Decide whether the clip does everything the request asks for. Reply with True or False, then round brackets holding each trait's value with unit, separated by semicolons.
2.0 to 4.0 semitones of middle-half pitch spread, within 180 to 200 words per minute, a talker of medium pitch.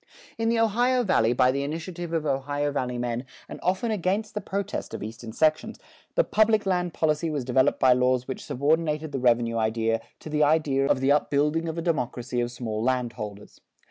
False (5.3 semitones; 190 wpm; 145 Hz)